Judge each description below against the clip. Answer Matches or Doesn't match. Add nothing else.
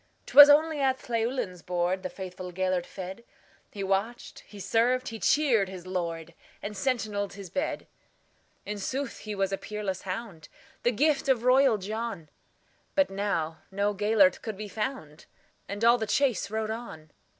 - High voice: Matches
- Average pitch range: Matches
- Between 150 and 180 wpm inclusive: Doesn't match